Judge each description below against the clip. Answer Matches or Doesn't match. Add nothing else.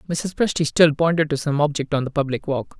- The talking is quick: Matches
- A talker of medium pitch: Matches